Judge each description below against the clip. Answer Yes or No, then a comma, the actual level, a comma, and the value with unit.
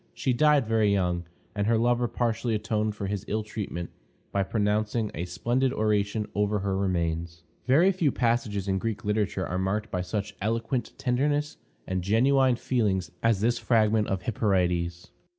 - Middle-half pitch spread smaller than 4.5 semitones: Yes, average, 3.5 semitones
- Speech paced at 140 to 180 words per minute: Yes, average, 160 wpm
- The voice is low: Yes, low, 105 Hz